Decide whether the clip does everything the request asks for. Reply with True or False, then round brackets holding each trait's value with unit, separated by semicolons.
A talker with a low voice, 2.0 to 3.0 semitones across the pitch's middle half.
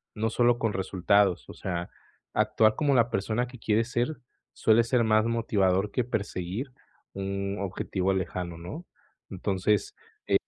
False (105 Hz; 3.4 semitones)